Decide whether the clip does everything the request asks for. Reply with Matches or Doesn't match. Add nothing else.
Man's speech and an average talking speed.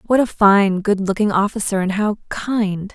Doesn't match